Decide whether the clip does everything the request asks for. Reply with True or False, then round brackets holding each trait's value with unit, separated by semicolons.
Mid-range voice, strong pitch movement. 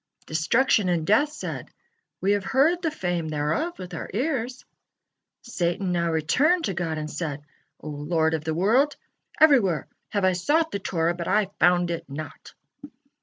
True (180 Hz; 7.7 semitones)